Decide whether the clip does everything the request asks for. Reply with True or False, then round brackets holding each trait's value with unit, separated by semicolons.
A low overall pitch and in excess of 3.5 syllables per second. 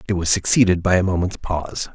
True (90 Hz; 6.3 syllables/s)